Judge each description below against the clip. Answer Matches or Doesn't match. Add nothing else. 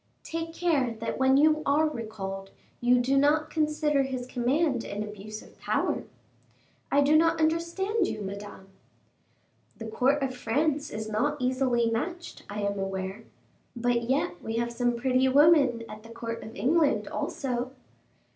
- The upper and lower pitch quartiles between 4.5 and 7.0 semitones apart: Matches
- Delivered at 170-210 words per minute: Doesn't match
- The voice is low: Doesn't match